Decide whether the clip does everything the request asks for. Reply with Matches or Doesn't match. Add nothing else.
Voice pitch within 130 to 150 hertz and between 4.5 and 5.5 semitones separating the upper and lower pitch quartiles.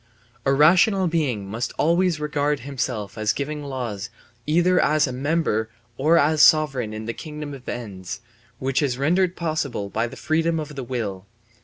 Matches